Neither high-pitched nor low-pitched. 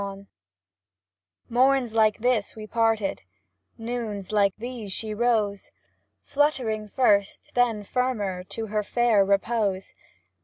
No: high, 215 Hz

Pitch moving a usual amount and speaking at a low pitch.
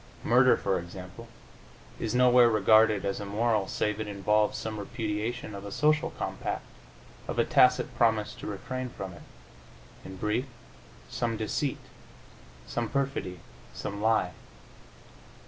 Yes: average, 3.1 semitones; low, 110 Hz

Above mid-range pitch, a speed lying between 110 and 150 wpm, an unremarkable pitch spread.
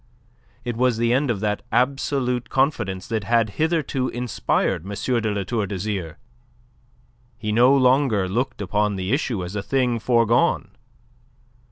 No: low, 115 Hz; average, 145 wpm; average, 3.7 semitones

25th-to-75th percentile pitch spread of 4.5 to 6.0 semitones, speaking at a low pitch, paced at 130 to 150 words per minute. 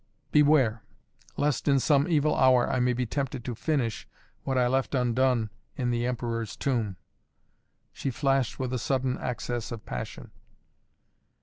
No: narrow, 2.4 semitones; low, 125 Hz; average, 145 wpm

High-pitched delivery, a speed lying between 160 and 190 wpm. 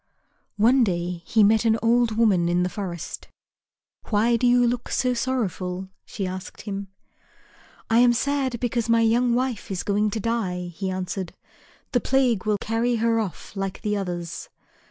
Yes: high, 220 Hz; average, 165 wpm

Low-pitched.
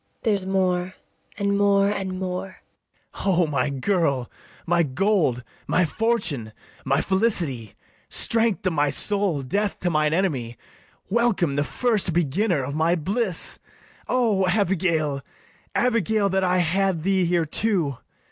No: medium, 185 Hz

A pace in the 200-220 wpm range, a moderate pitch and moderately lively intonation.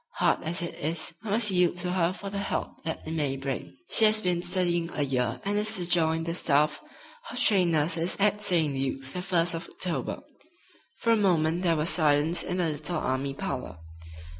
Yes: fast, 205 wpm; medium, 170 Hz; average, 3.5 semitones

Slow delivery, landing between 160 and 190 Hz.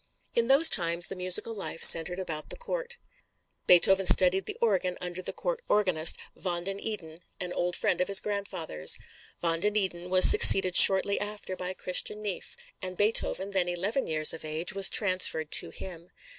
No: average, 175 wpm; medium, 185 Hz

